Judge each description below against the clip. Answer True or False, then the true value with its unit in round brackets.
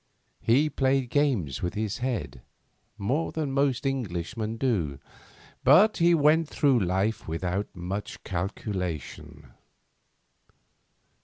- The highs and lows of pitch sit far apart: True (7.1 semitones)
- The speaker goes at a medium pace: False (100 wpm)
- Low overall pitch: True (115 Hz)